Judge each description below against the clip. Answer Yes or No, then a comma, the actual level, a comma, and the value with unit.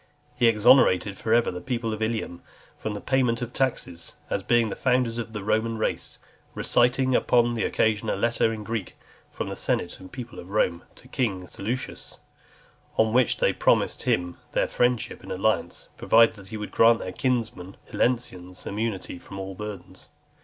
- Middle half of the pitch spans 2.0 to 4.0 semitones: Yes, average, 3.6 semitones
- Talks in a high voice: No, low, 110 Hz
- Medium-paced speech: Yes, average, 180 wpm